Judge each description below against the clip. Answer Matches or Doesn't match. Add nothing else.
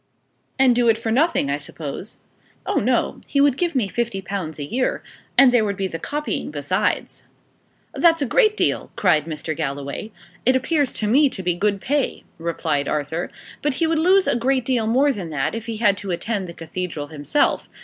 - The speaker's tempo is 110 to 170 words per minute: Doesn't match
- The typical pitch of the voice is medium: Doesn't match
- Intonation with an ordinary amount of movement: Doesn't match